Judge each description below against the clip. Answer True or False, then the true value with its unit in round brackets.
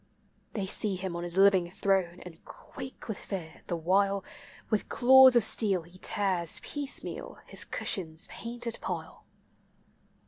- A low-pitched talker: False (195 Hz)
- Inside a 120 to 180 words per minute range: True (140 wpm)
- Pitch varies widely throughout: False (3.8 semitones)